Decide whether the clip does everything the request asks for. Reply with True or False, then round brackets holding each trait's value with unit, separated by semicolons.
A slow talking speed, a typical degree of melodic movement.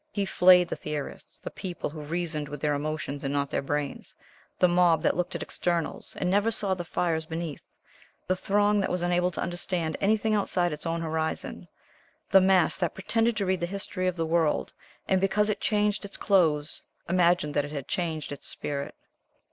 False (195 wpm; 3.6 semitones)